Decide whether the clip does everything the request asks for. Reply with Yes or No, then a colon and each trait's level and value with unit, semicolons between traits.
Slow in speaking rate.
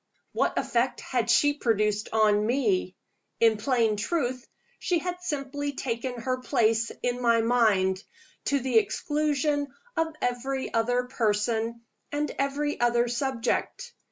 Yes: slow, 130 wpm